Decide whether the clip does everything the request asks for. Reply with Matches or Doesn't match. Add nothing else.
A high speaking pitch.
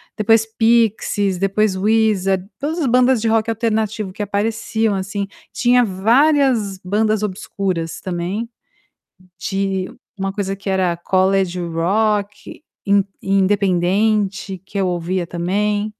Matches